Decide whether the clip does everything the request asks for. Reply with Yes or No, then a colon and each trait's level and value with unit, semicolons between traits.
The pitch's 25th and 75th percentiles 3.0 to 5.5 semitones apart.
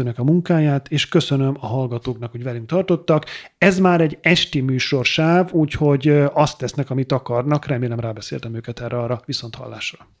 Yes: average, 4.6 semitones